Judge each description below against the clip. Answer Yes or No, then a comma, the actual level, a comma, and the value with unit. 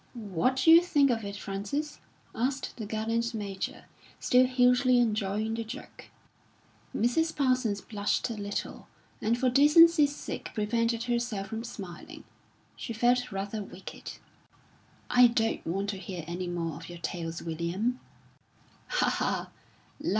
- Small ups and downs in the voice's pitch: No, average, 4.1 semitones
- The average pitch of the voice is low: No, high, 225 Hz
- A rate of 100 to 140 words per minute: Yes, slow, 135 wpm